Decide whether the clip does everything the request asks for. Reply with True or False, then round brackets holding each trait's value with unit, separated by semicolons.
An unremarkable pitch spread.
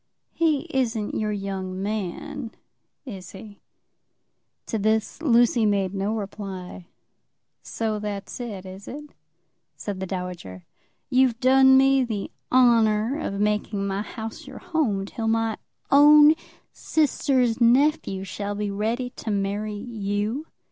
True (4.2 semitones)